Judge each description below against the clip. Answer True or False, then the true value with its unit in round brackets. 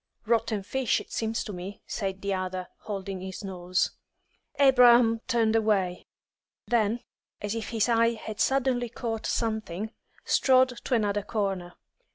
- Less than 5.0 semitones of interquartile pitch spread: True (3.3 semitones)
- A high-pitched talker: True (220 Hz)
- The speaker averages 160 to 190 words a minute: False (140 wpm)